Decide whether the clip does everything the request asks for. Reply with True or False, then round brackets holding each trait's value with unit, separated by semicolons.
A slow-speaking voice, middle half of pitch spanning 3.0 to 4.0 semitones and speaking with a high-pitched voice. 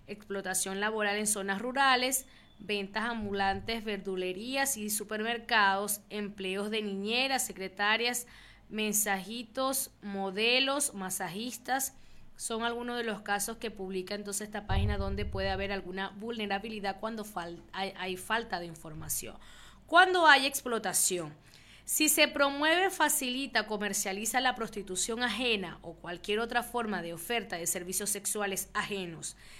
True (120 wpm; 3.7 semitones; 210 Hz)